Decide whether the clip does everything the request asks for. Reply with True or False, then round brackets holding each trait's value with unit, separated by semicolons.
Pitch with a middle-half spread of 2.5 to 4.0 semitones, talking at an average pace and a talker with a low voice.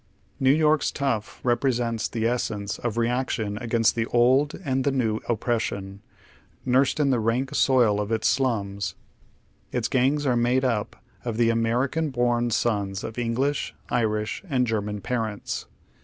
True (2.9 semitones; 145 wpm; 120 Hz)